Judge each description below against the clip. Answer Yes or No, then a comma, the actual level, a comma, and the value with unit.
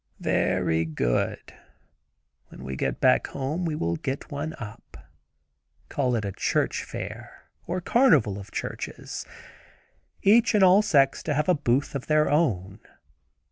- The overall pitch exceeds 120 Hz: Yes, medium, 140 Hz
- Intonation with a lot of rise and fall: Yes, wide, 8.7 semitones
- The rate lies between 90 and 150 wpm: Yes, average, 140 wpm